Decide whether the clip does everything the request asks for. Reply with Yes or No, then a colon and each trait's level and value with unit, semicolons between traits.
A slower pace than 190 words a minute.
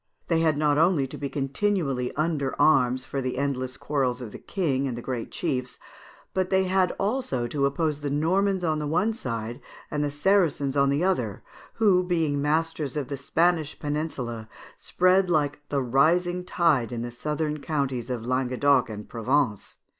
Yes: average, 170 wpm